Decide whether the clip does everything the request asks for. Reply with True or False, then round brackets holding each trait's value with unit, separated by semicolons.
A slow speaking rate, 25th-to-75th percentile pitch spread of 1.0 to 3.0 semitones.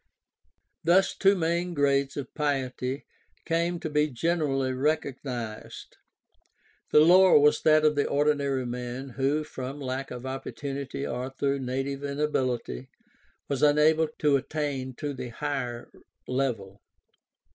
True (125 wpm; 2.6 semitones)